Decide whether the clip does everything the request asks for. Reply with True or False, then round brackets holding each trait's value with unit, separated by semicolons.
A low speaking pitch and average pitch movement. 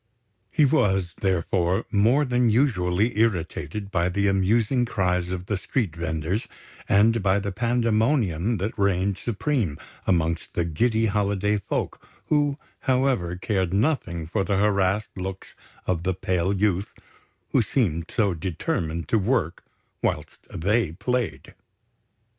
True (100 Hz; 4.2 semitones)